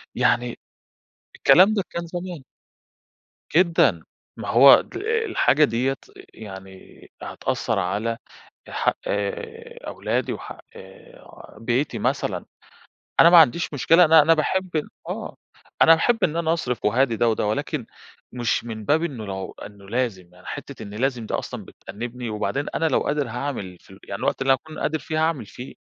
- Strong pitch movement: Yes, wide, 6.6 semitones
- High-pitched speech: No, low, 130 Hz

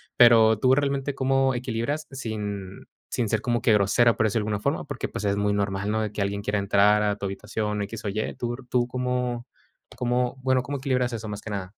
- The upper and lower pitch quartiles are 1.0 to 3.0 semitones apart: No, average, 3.5 semitones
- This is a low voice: Yes, low, 110 Hz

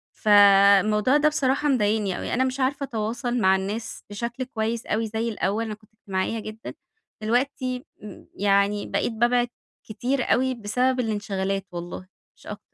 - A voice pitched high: Yes, high, 220 Hz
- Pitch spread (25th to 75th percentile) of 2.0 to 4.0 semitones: Yes, average, 3.5 semitones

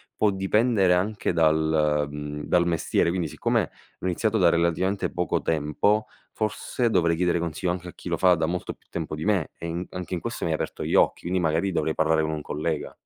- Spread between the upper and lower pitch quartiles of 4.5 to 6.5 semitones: No, average, 2.9 semitones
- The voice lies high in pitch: No, very low, 85 Hz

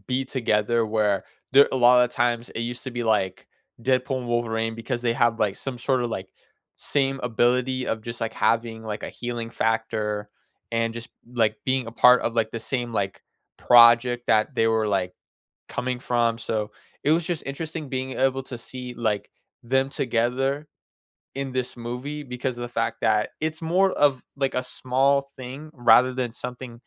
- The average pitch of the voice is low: Yes, low, 120 Hz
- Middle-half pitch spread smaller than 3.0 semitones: Yes, narrow, 2.4 semitones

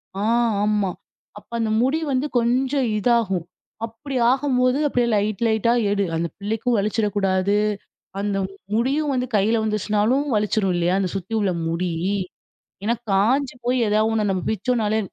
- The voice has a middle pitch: No, high, 215 Hz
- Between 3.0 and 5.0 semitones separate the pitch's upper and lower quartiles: Yes, average, 3.7 semitones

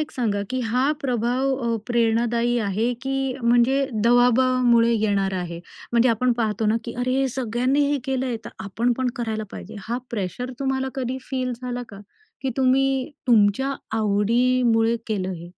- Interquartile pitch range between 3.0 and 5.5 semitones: No, narrow, 2.5 semitones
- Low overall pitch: No, high, 240 Hz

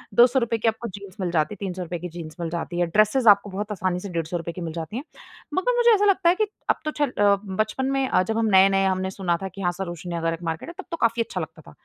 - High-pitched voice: Yes, high, 195 Hz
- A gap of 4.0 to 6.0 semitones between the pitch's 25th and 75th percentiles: Yes, average, 4.8 semitones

